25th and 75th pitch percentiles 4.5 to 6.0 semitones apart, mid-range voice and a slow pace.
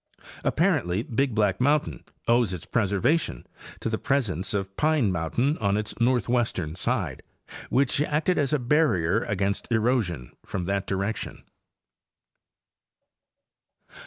No: average, 5.3 semitones; low, 110 Hz; slow, 120 wpm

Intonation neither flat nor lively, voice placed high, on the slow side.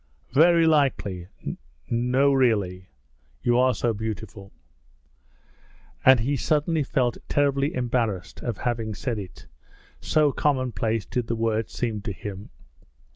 No: average, 4.0 semitones; low, 120 Hz; slow, 120 wpm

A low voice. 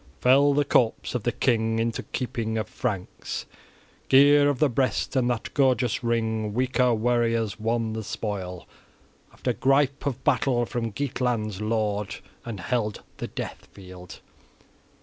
Yes: low, 115 Hz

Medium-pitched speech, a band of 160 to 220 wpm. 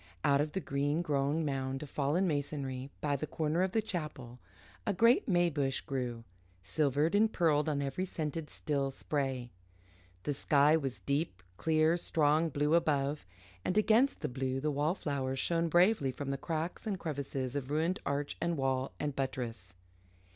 Yes: medium, 145 Hz; average, 165 wpm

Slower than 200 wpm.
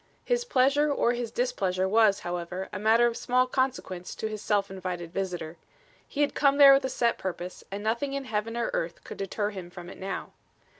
No: fast, 205 wpm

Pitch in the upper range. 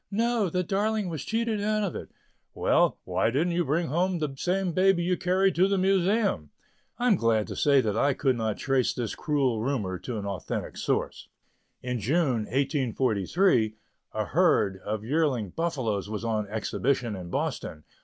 No: medium, 140 Hz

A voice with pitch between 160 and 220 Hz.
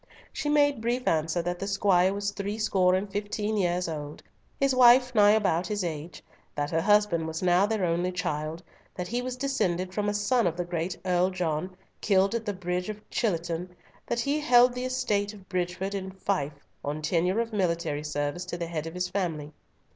Yes: medium, 185 Hz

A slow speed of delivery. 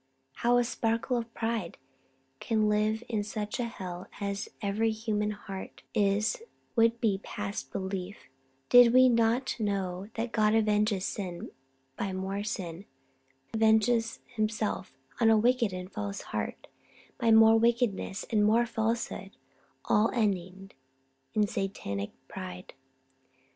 Yes: slow, 130 wpm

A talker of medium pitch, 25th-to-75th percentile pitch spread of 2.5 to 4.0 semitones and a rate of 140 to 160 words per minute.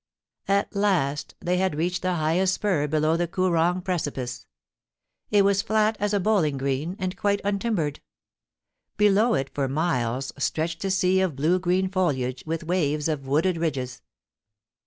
No: medium, 175 Hz; average, 4.4 semitones; average, 155 wpm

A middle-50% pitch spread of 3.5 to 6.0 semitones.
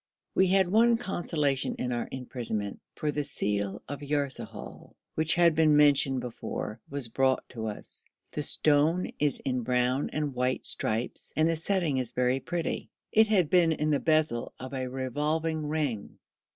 Yes: average, 4.0 semitones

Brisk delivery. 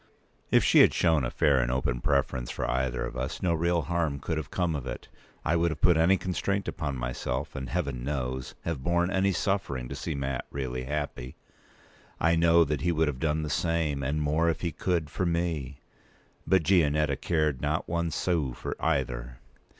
No: average, 195 wpm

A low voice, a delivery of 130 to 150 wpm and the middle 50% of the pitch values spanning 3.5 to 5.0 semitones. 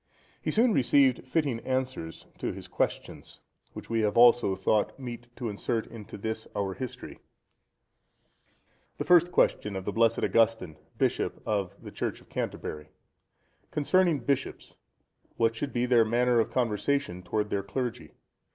Yes: low, 115 Hz; average, 140 wpm; average, 3.8 semitones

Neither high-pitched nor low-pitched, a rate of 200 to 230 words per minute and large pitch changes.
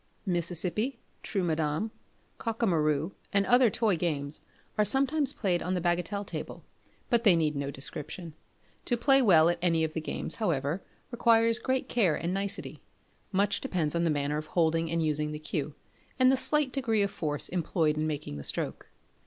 No: medium, 175 Hz; average, 175 wpm; wide, 6.3 semitones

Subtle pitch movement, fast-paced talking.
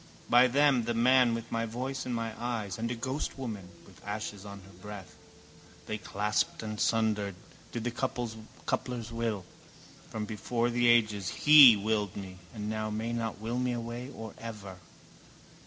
No: narrow, 2.3 semitones; average, 160 wpm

